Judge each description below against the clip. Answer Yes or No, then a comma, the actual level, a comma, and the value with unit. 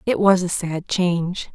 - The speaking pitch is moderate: Yes, medium, 180 Hz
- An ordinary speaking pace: Yes, average, 195 wpm